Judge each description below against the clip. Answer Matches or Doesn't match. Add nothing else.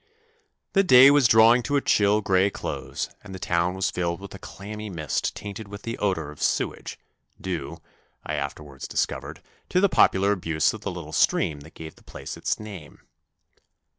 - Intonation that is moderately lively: Matches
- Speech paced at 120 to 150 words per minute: Doesn't match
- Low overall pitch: Matches